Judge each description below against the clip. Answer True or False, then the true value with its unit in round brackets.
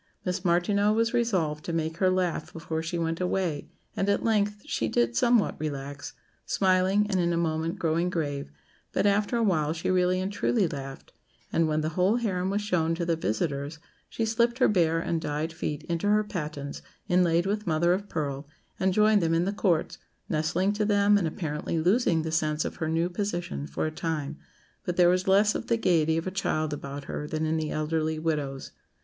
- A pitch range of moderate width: True (3.9 semitones)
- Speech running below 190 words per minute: False (200 wpm)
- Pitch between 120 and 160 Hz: False (170 Hz)